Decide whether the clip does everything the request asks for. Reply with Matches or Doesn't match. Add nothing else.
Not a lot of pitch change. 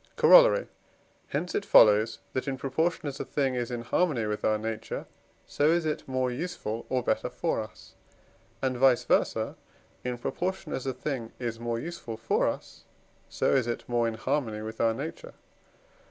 Doesn't match